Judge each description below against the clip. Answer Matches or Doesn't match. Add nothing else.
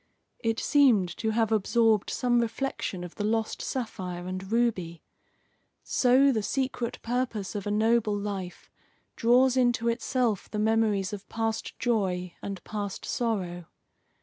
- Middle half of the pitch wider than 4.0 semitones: Doesn't match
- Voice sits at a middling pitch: Doesn't match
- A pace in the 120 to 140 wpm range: Matches